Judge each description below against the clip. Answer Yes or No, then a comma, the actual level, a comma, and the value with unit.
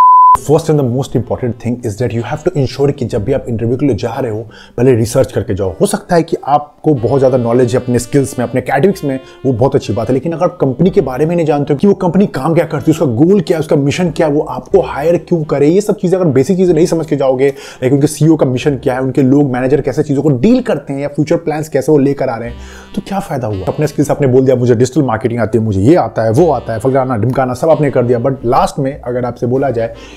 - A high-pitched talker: No, medium, 140 Hz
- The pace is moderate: No, fast, 290 wpm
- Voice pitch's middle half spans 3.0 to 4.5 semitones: Yes, average, 4.1 semitones